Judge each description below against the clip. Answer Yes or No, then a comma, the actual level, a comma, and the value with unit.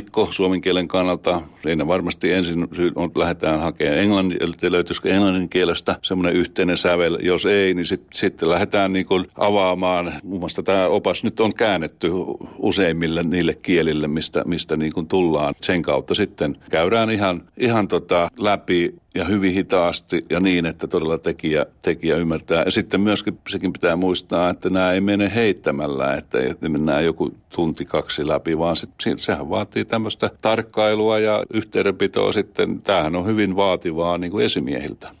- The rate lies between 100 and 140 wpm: No, fast, 155 wpm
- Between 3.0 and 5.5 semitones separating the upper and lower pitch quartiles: No, narrow, 2.6 semitones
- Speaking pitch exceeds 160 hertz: No, very low, 90 Hz